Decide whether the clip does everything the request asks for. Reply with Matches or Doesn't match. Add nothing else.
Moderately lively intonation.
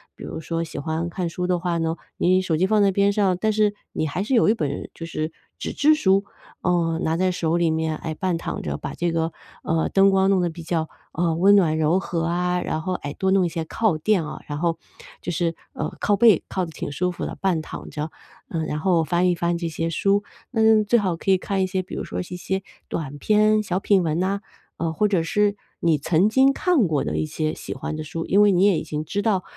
Matches